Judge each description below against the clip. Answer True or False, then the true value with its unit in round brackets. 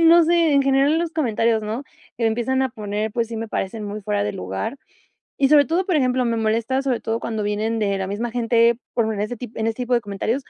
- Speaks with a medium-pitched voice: False (230 Hz)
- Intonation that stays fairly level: False (3.5 semitones)